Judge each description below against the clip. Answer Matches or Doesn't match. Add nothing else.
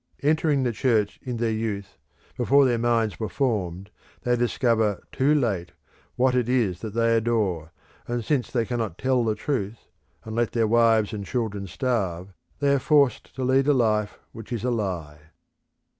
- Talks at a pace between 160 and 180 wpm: Matches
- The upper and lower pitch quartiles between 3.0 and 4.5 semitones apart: Matches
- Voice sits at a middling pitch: Doesn't match